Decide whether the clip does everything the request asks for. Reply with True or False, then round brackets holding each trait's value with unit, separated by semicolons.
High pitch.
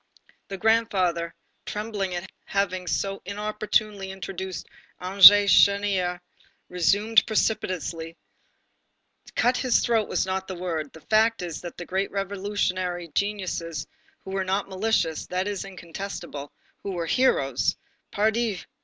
True (195 Hz)